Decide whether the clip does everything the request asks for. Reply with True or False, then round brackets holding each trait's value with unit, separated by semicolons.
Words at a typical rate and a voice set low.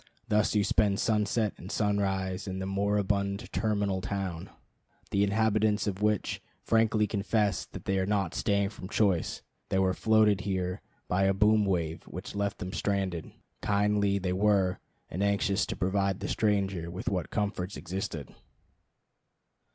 True (150 wpm; 100 Hz)